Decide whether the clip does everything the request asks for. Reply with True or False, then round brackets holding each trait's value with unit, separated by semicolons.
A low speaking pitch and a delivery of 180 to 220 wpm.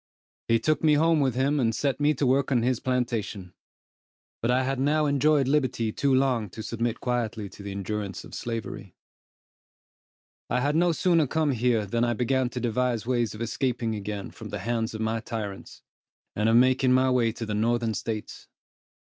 True (120 Hz; 190 wpm)